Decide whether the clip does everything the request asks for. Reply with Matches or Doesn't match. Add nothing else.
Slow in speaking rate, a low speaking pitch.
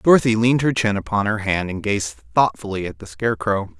Doesn't match